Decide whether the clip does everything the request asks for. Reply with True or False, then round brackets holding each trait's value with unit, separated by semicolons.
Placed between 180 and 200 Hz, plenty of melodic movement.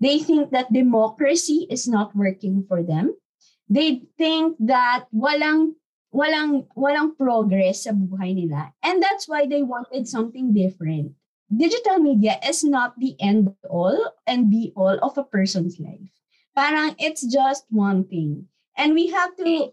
False (250 Hz; 7.3 semitones)